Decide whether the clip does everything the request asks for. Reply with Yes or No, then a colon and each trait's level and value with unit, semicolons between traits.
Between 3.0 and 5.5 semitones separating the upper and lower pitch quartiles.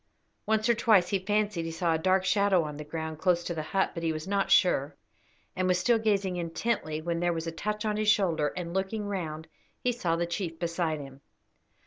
Yes: average, 3.8 semitones